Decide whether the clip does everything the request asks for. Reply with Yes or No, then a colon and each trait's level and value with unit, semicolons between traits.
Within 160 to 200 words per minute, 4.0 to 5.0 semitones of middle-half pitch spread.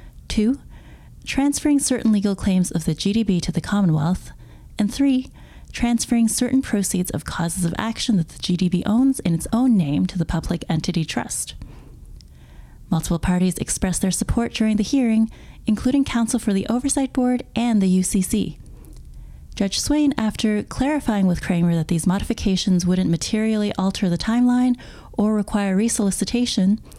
No: average, 150 wpm; average, 4.7 semitones